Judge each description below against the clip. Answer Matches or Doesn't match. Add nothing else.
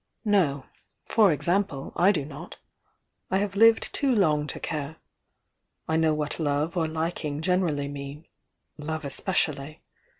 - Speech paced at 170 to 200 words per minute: Doesn't match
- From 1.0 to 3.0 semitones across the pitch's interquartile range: Doesn't match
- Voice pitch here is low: Doesn't match